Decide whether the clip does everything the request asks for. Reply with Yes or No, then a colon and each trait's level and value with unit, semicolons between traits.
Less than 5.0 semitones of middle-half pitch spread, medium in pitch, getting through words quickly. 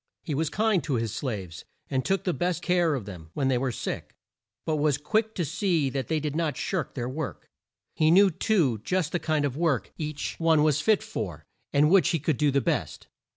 Yes: average, 4.6 semitones; medium, 155 Hz; fast, 225 wpm